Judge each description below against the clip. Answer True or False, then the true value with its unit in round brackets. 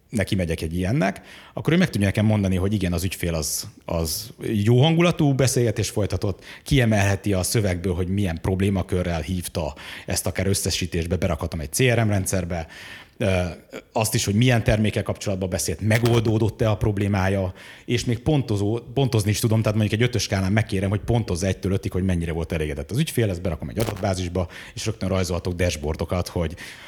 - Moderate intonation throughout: True (3.4 semitones)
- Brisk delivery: True (165 wpm)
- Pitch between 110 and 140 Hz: False (100 Hz)